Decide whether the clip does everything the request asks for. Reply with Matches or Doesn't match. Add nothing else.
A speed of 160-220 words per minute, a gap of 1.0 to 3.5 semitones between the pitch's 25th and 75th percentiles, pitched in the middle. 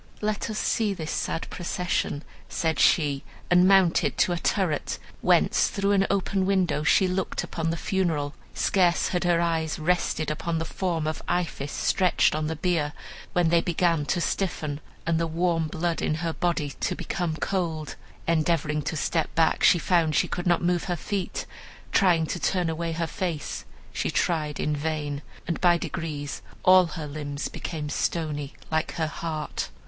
Matches